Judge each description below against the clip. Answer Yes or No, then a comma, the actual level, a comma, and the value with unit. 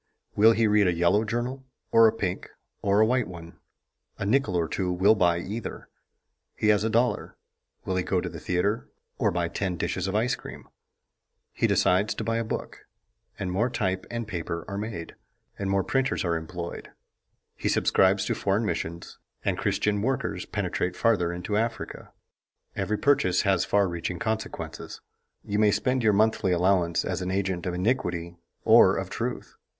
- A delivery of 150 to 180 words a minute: Yes, average, 175 wpm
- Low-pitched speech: Yes, low, 100 Hz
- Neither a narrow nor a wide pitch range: Yes, average, 3.7 semitones